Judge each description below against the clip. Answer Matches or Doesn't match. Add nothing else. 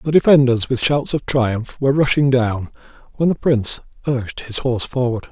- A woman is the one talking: Doesn't match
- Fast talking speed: Doesn't match